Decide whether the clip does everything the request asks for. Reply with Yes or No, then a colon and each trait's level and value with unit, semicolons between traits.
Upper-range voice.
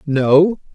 No: medium, 155 Hz